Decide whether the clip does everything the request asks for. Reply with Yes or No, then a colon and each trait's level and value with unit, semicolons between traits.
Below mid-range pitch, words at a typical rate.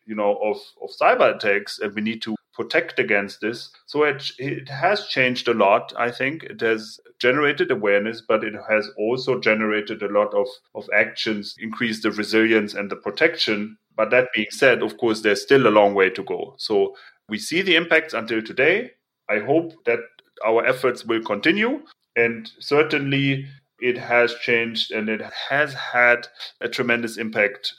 Yes: low, 115 Hz; average, 175 wpm